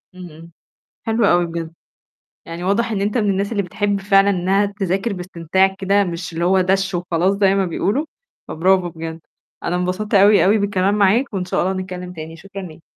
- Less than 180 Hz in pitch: No, high, 190 Hz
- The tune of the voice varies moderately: No, narrow, 2.3 semitones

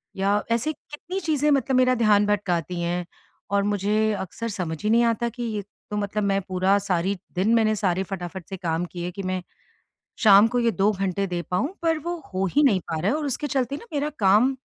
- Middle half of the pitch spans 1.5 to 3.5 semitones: No, average, 4.2 semitones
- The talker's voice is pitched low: No, high, 205 Hz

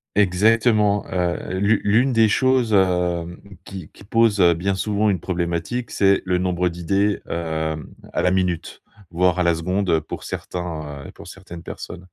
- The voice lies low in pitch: Yes, very low, 90 Hz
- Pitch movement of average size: Yes, average, 3.1 semitones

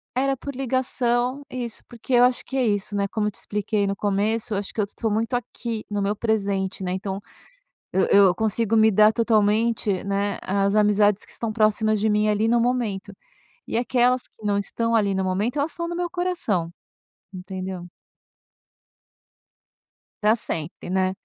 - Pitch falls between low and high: No, high, 215 Hz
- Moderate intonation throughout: Yes, average, 3.1 semitones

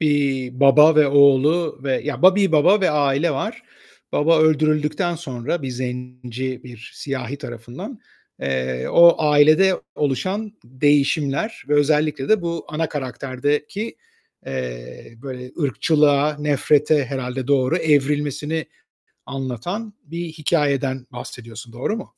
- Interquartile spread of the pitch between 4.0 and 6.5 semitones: No, average, 3.5 semitones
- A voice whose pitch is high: No, medium, 145 Hz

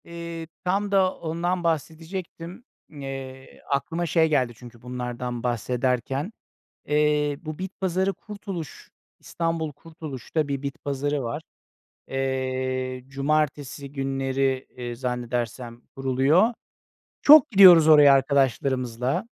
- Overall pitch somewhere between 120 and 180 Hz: Yes, medium, 140 Hz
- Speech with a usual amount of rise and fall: Yes, average, 4.2 semitones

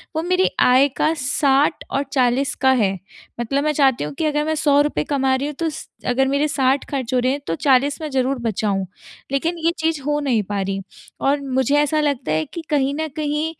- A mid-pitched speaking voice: No, very high, 275 Hz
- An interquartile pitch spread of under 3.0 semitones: Yes, narrow, 2.6 semitones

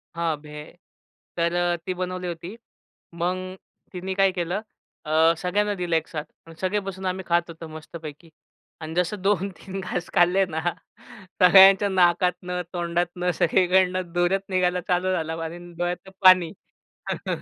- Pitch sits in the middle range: Yes, medium, 180 Hz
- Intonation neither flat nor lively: No, narrow, 1.7 semitones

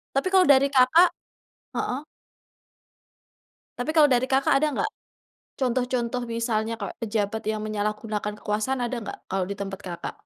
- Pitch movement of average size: Yes, average, 3.8 semitones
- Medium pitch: No, high, 235 Hz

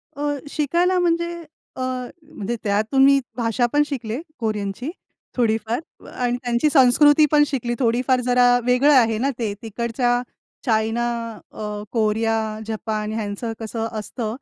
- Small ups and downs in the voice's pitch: No, average, 3.7 semitones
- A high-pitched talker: Yes, high, 240 Hz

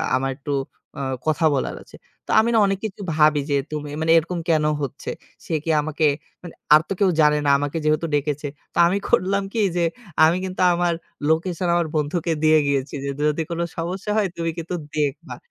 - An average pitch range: Yes, average, 3.0 semitones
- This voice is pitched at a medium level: Yes, medium, 160 Hz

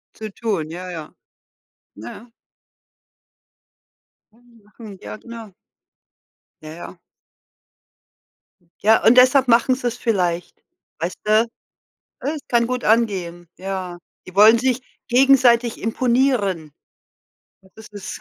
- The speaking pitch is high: Yes, high, 220 Hz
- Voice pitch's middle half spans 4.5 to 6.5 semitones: Yes, average, 4.8 semitones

